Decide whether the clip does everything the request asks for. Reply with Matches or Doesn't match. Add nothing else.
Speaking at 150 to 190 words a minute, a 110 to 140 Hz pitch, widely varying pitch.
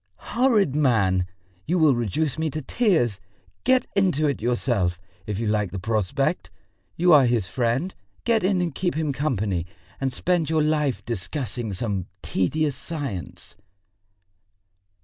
Doesn't match